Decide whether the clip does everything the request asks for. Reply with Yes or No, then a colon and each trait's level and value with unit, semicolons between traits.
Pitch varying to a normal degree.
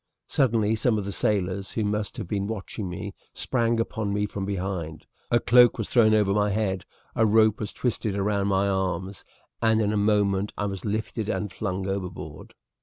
No: narrow, 2.1 semitones